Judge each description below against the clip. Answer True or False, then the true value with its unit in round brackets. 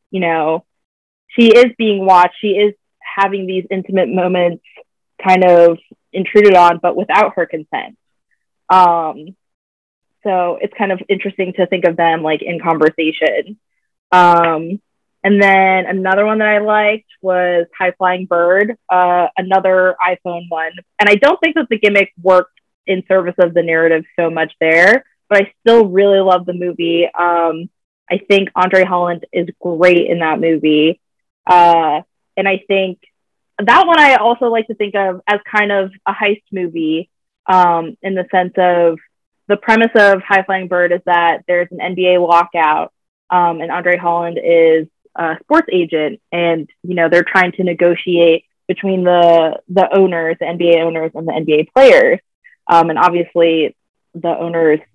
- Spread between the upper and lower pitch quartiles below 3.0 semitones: True (2.5 semitones)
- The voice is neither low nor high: True (180 Hz)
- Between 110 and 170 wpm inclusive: True (160 wpm)